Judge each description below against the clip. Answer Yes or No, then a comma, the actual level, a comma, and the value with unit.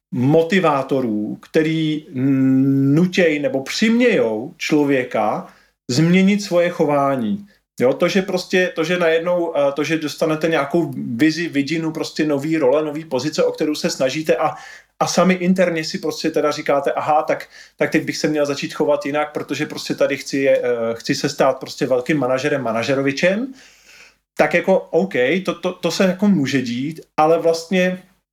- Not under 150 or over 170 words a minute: Yes, average, 155 wpm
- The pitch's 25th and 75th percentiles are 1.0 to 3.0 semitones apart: No, average, 3.5 semitones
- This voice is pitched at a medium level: Yes, medium, 160 Hz